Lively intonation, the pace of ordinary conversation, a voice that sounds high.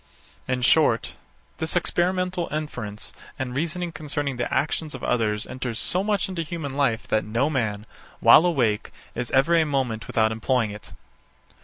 No: wide, 6.1 semitones; average, 155 wpm; low, 135 Hz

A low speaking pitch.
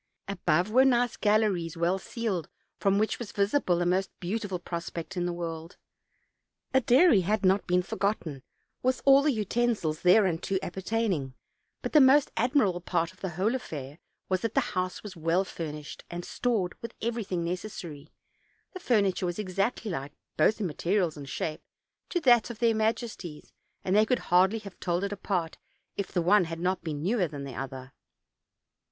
No: high, 190 Hz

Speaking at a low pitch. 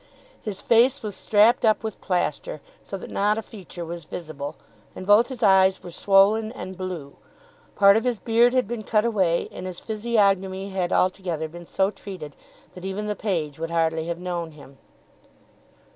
No: high, 190 Hz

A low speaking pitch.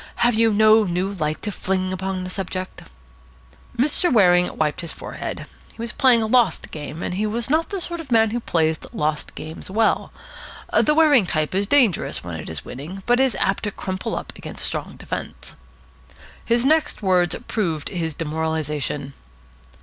No: high, 190 Hz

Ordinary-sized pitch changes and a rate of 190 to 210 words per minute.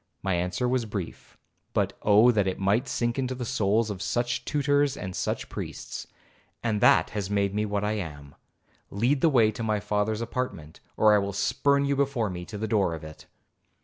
Yes: average, 3.8 semitones; average, 200 wpm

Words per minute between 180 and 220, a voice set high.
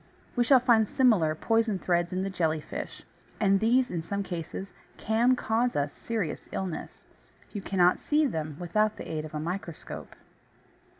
No: average, 165 wpm; high, 195 Hz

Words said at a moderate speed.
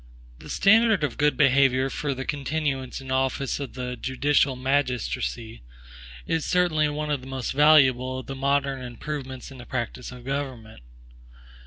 Yes: average, 155 wpm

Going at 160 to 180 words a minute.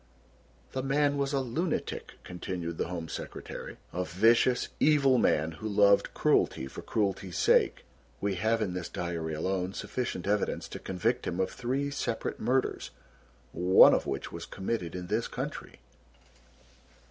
No: average, 145 wpm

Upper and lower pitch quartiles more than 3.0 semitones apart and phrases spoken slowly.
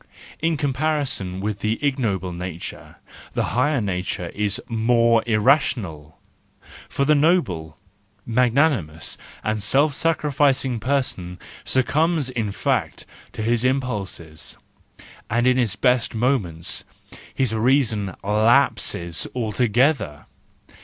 Yes: wide, 5.6 semitones; slow, 105 wpm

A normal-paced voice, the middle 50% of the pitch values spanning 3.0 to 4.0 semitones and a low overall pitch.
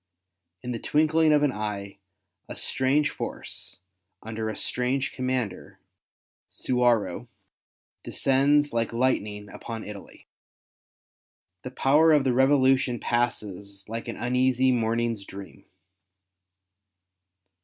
No: slow, 100 wpm; average, 3.4 semitones; low, 125 Hz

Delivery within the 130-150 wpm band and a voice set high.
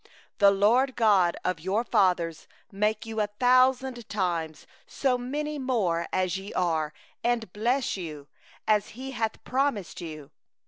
Yes: average, 145 wpm; high, 210 Hz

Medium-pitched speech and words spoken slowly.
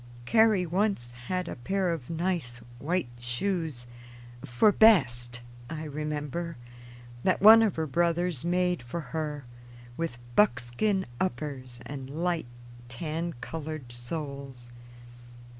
Yes: medium, 155 Hz; slow, 110 wpm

